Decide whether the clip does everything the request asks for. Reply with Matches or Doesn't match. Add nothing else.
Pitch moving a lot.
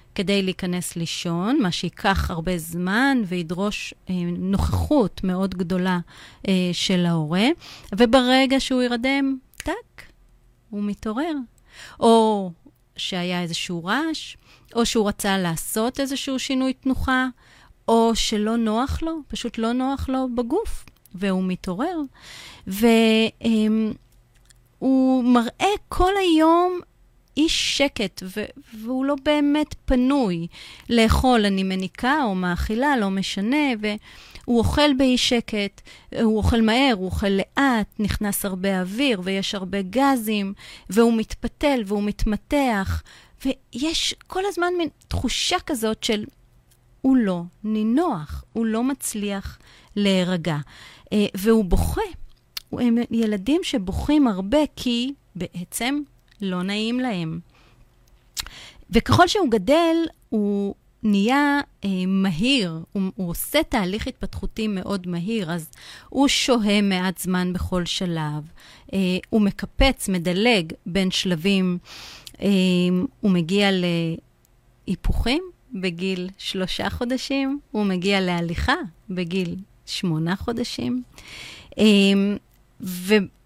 Matches